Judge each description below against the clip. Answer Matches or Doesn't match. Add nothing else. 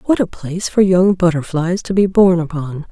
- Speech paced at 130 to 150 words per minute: Doesn't match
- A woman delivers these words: Matches